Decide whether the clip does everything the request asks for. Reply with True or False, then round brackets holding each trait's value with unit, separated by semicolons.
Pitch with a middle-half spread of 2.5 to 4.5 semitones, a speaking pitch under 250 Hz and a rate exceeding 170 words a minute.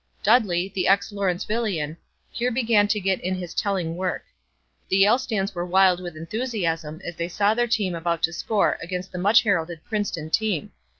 True (3.5 semitones; 190 Hz; 180 wpm)